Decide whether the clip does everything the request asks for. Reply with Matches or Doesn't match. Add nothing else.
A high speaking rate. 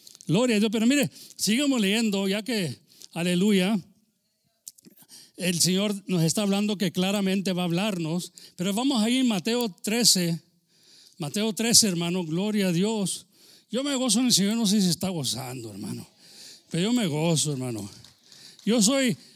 Doesn't match